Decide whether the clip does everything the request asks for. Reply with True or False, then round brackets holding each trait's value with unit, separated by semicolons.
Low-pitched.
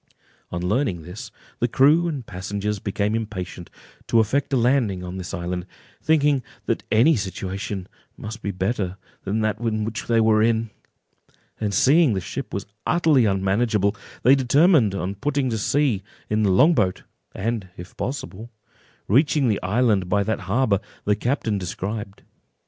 True (110 Hz)